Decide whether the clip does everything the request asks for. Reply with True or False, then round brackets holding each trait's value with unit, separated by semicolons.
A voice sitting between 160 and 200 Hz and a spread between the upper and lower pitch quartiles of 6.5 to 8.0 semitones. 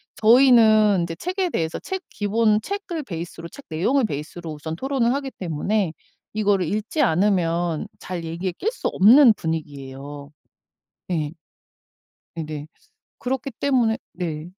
True (190 Hz; 7.0 semitones)